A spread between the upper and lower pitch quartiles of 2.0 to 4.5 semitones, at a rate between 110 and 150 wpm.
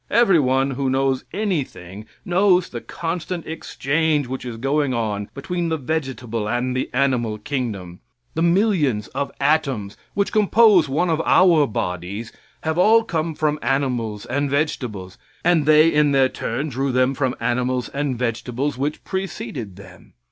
No: average, 4.9 semitones; average, 145 wpm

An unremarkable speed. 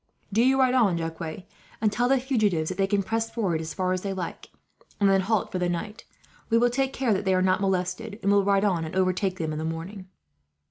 No: fast, 245 wpm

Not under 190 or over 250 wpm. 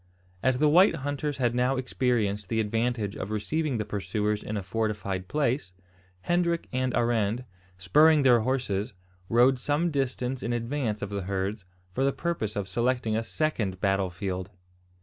No: average, 160 wpm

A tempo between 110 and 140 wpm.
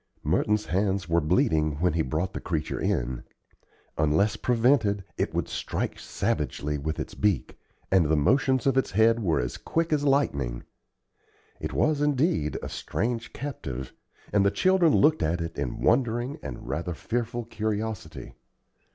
No: average, 150 wpm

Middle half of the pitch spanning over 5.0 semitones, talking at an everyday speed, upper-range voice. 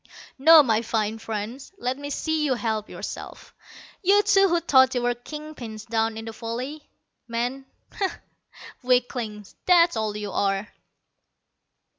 Yes: wide, 5.4 semitones; average, 145 wpm; high, 245 Hz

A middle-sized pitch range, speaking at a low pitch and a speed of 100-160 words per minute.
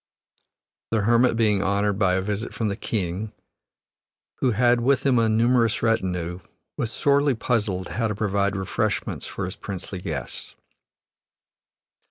Yes: average, 3.4 semitones; low, 105 Hz; average, 140 wpm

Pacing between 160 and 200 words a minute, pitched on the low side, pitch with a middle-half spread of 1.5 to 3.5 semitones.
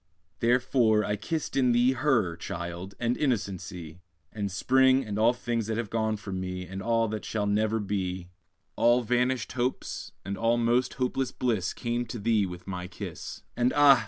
No: average, 170 wpm; low, 110 Hz; average, 3.9 semitones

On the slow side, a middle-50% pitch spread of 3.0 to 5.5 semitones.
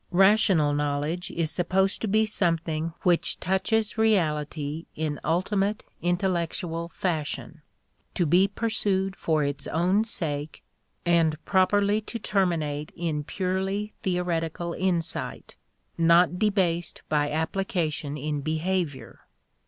Yes: slow, 105 wpm; average, 3.5 semitones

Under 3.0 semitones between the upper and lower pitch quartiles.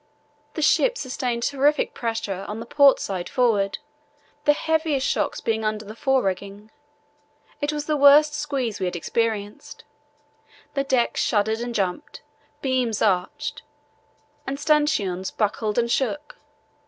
No: wide, 5.4 semitones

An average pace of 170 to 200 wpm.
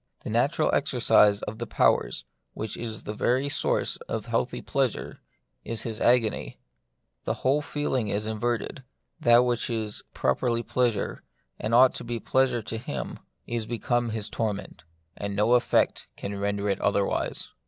No: average, 160 wpm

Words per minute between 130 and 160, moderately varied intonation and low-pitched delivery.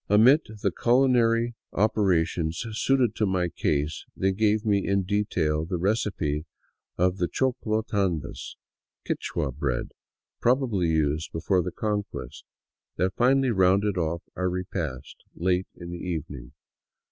Yes: slow, 135 wpm; average, 4.5 semitones; very low, 95 Hz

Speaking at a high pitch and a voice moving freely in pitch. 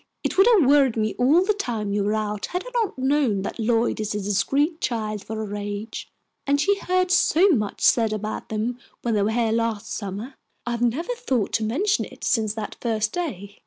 Yes: high, 230 Hz; wide, 5.8 semitones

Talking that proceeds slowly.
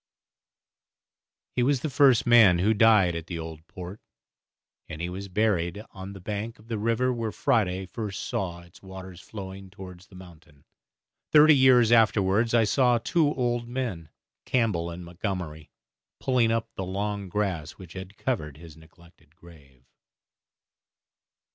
No: average, 150 wpm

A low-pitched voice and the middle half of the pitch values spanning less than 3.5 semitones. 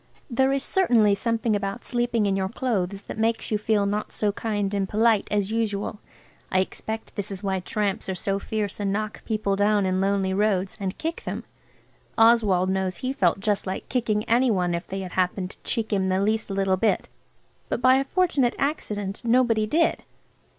No: high, 210 Hz; average, 2.8 semitones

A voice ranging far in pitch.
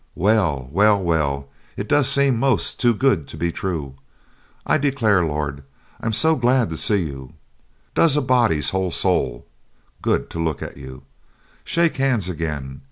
Yes: wide, 8.6 semitones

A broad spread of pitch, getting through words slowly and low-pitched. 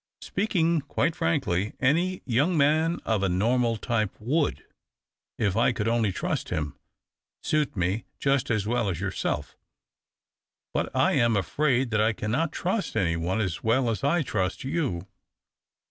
No: wide, 6.4 semitones; average, 155 wpm; low, 115 Hz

